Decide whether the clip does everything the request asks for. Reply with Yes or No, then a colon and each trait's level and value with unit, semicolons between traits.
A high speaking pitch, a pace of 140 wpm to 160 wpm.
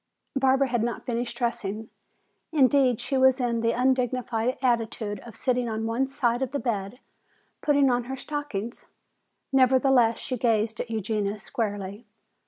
Yes: high, 240 Hz; average, 145 wpm